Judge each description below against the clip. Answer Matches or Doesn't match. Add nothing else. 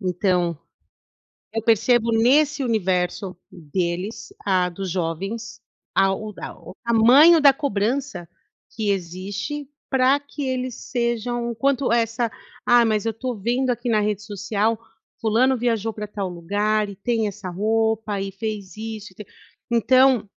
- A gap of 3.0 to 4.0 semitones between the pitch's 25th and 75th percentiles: Matches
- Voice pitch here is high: Matches